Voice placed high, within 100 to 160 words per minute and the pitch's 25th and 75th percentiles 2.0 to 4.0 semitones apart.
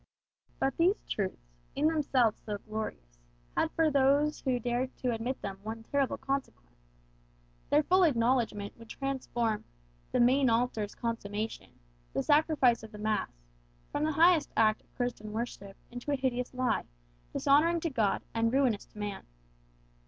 No: high, 245 Hz; average, 150 wpm; average, 4.4 semitones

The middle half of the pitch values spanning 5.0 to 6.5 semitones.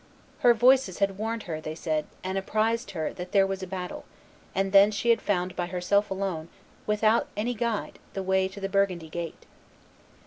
No: average, 3.0 semitones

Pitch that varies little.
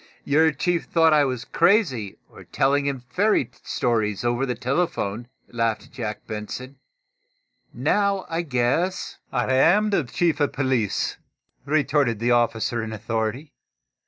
No: wide, 5.4 semitones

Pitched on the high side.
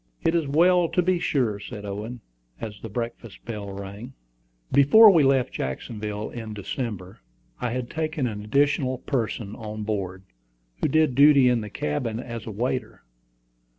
No: low, 120 Hz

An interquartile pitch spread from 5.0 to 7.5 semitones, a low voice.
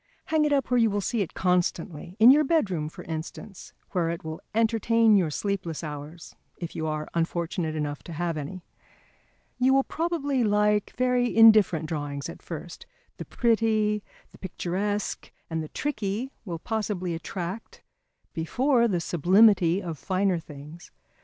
No: wide, 5.5 semitones; high, 190 Hz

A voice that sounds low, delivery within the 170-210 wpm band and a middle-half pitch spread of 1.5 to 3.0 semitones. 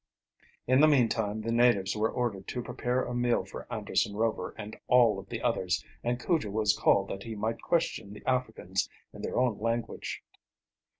Yes: low, 115 Hz; average, 180 wpm; average, 2.7 semitones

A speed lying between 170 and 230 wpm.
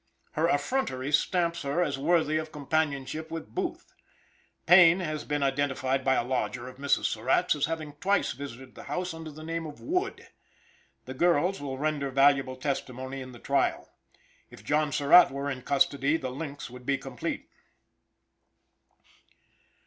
No: average, 155 wpm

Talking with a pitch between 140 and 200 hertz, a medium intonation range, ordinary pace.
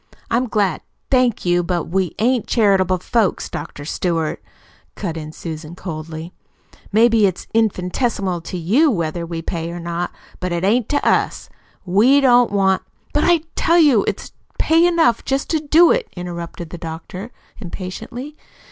No: high, 190 Hz; wide, 6.0 semitones; average, 160 wpm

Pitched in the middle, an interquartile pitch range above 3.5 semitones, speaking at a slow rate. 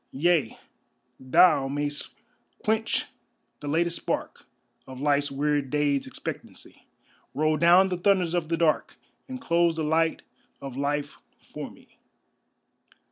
No: medium, 155 Hz; average, 3.2 semitones; slow, 125 wpm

